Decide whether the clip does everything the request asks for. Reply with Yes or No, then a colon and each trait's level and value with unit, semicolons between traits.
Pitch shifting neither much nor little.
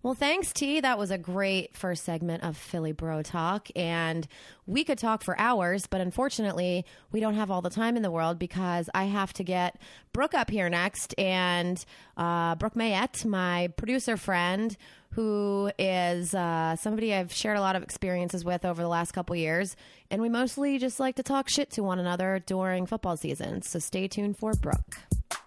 Yes: average, 3.7 semitones